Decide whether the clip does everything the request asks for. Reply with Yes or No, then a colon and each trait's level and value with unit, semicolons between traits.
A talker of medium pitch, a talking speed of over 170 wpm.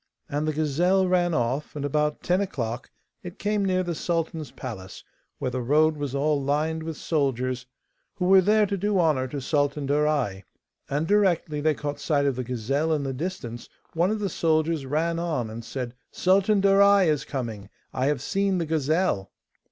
Yes: medium, 155 Hz; average, 185 wpm